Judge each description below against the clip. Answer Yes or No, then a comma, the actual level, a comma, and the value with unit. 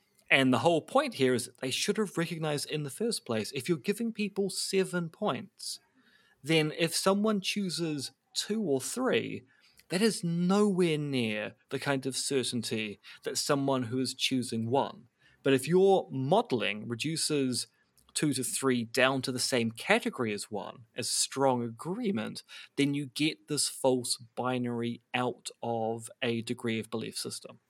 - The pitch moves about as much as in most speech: No, wide, 5.8 semitones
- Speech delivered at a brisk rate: No, average, 160 wpm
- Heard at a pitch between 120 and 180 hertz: Yes, low, 135 Hz